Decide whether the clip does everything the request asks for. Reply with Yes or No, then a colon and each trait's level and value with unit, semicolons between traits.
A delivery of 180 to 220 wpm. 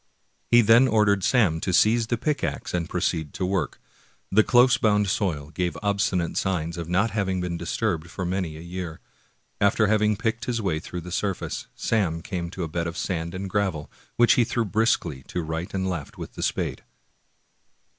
Yes: average, 190 wpm